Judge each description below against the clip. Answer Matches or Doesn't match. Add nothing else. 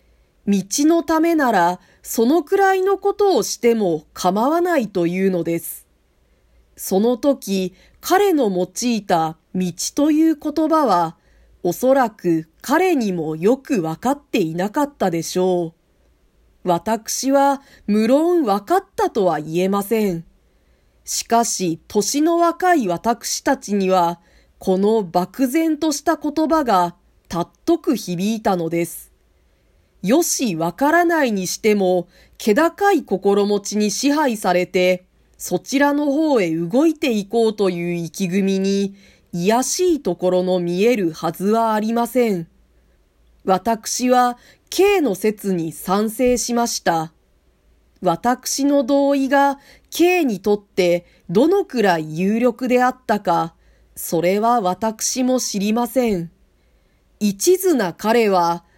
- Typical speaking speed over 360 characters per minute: Doesn't match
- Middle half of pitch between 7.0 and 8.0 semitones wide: Matches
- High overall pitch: Matches